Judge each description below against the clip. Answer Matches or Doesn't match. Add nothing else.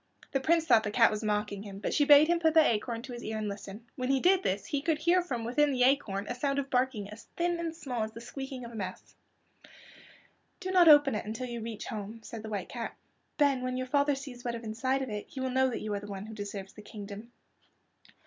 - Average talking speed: Doesn't match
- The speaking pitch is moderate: Doesn't match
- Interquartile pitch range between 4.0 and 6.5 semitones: Matches